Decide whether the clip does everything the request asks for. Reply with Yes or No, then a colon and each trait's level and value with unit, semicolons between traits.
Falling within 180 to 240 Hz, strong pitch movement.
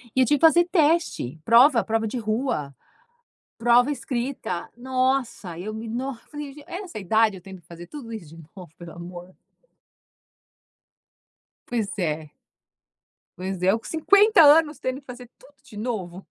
Yes: high, 230 Hz; wide, 6.9 semitones